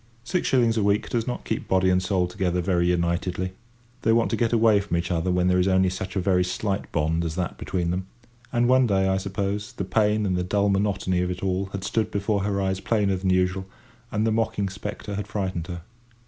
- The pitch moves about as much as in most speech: No, narrow, 2.2 semitones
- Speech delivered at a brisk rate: Yes, fast, 230 wpm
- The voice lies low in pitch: Yes, very low, 95 Hz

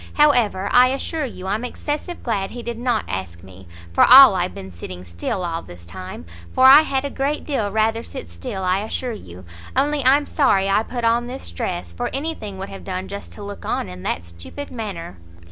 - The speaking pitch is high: Yes, high, 205 Hz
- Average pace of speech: No, fast, 215 wpm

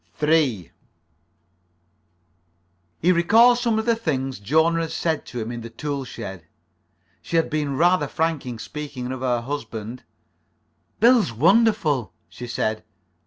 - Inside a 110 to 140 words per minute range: Yes, slow, 135 wpm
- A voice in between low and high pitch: Yes, medium, 145 Hz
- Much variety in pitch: Yes, wide, 5.7 semitones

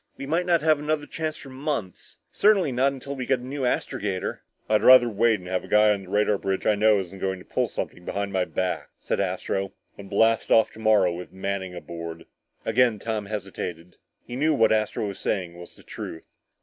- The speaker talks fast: Yes, fast, 210 wpm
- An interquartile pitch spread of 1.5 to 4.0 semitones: No, average, 5.3 semitones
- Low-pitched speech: Yes, low, 105 Hz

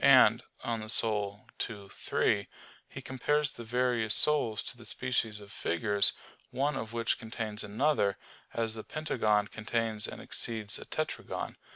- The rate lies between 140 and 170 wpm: Yes, average, 145 wpm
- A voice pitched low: Yes, low, 110 Hz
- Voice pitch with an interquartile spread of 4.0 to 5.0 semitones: No, average, 2.9 semitones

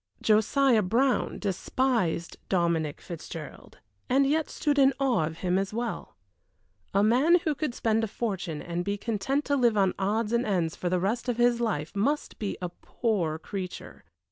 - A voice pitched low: No, high, 215 Hz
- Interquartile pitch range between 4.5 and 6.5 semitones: Yes, wide, 5.5 semitones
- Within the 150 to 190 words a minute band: Yes, average, 170 wpm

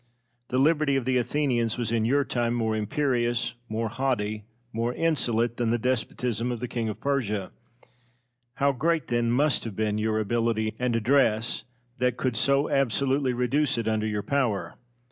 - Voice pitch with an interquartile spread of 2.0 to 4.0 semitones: Yes, average, 3.3 semitones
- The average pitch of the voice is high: No, low, 120 Hz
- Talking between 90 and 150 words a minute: No, average, 165 wpm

